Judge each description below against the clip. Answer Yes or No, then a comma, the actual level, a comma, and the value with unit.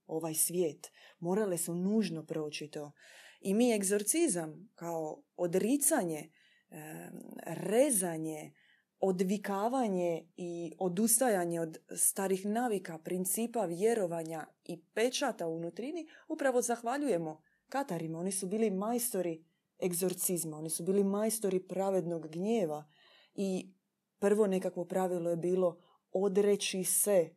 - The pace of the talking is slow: Yes, slow, 105 wpm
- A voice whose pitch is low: No, medium, 185 Hz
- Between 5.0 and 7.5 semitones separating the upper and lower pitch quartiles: No, average, 4.2 semitones